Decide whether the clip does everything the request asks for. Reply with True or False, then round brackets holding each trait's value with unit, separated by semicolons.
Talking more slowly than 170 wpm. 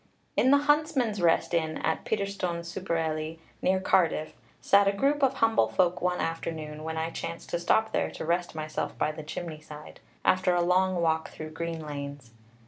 False (185 wpm)